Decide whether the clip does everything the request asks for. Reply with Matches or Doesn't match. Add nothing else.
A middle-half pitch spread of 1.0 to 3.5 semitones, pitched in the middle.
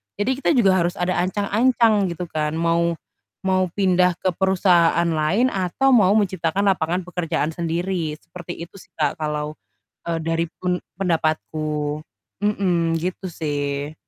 Matches